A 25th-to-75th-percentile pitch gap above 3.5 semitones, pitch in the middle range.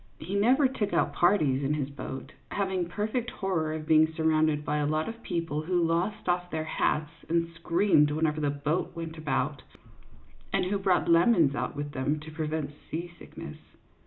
No: average, 3.1 semitones; medium, 160 Hz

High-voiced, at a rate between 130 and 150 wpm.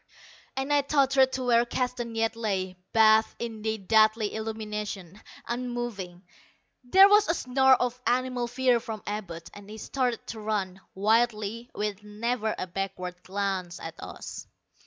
Yes: high, 220 Hz; average, 145 wpm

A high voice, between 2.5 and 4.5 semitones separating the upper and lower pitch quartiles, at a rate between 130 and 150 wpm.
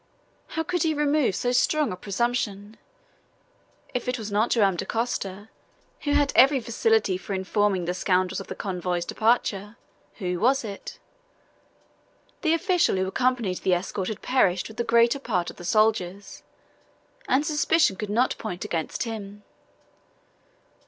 No: high, 215 Hz; average, 4.9 semitones; average, 145 wpm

